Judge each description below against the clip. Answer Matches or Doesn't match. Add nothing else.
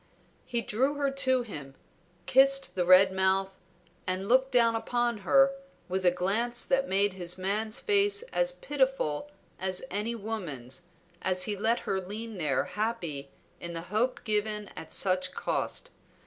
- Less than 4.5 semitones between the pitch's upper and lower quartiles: Doesn't match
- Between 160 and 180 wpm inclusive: Doesn't match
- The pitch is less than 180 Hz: Doesn't match